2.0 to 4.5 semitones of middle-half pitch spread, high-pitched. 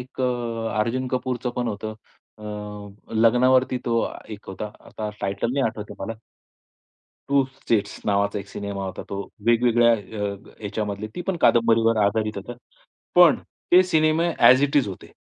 No: average, 3.6 semitones; low, 115 Hz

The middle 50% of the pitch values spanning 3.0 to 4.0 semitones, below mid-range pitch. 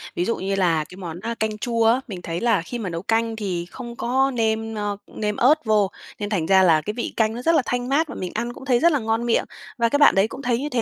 No: average, 3.7 semitones; high, 225 Hz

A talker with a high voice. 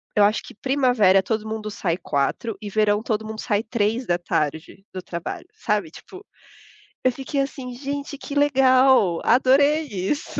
Yes: high, 220 Hz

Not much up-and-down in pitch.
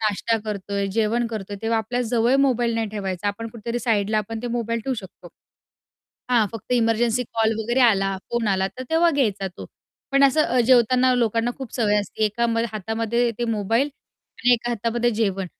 Yes: narrow, 2.3 semitones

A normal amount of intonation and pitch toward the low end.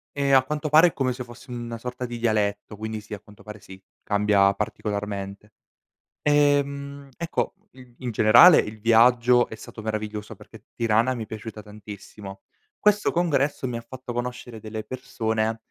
Yes: average, 3.4 semitones; low, 115 Hz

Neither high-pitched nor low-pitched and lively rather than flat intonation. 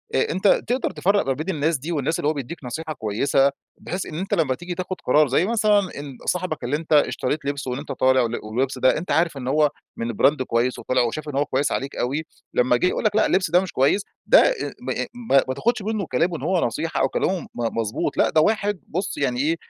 Yes: medium, 150 Hz; wide, 5.7 semitones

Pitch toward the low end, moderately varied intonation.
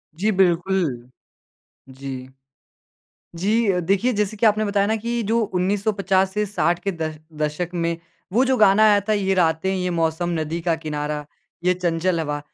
No: medium, 185 Hz; average, 4.0 semitones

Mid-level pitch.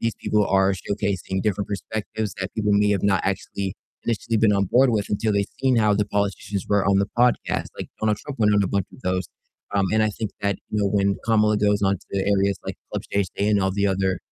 No: low, 100 Hz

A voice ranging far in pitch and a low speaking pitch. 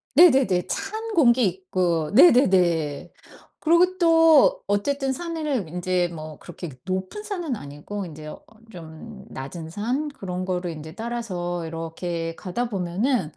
No: wide, 7.9 semitones; high, 190 Hz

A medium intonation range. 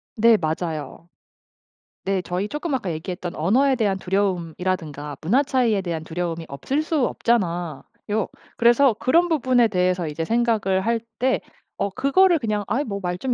No: wide, 6.0 semitones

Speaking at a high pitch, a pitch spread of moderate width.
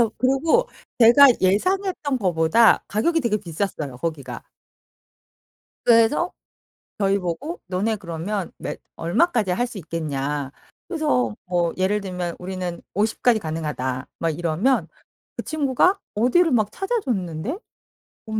No: high, 200 Hz; wide, 7.3 semitones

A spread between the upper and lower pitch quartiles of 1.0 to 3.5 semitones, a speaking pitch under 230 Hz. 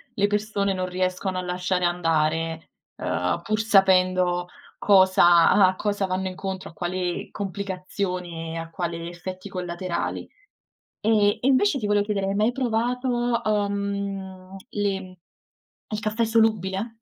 Yes: narrow, 2.5 semitones; high, 190 Hz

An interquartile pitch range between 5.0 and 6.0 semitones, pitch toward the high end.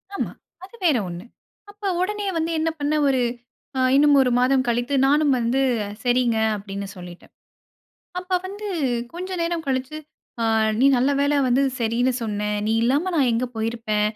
Yes: wide, 5.6 semitones; very high, 260 Hz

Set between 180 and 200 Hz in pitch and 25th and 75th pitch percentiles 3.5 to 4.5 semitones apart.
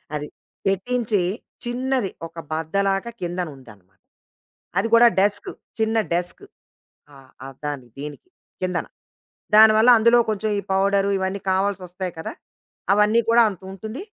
Yes: high, 195 Hz; average, 3.9 semitones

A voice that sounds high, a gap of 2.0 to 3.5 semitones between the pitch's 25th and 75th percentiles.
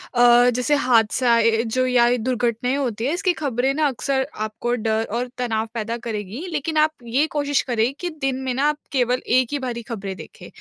Yes: high, 245 Hz; average, 2.9 semitones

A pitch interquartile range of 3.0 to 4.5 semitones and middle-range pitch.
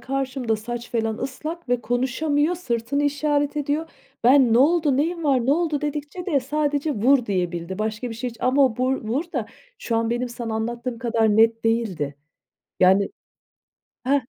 No: average, 4.2 semitones; very high, 255 Hz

